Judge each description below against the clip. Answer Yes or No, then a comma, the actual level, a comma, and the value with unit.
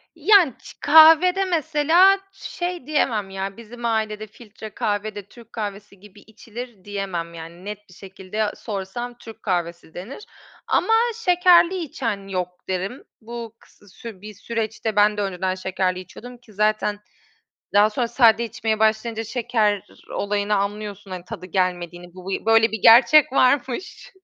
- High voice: Yes, high, 215 Hz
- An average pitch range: Yes, average, 3.7 semitones